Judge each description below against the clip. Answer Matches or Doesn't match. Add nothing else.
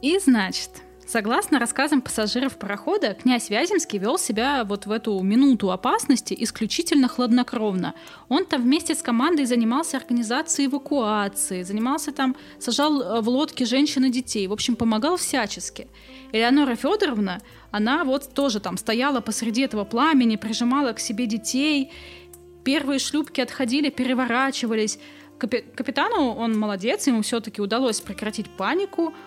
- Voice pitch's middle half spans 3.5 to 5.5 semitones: Matches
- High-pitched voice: Matches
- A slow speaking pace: Doesn't match